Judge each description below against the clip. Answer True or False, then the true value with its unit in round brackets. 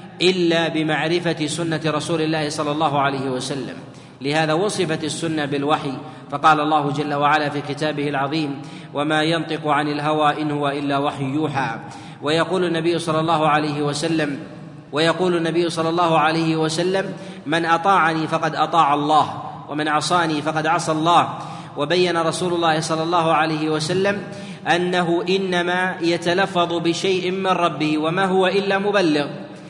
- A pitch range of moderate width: False (2.3 semitones)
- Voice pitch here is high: False (160 Hz)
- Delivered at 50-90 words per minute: False (135 wpm)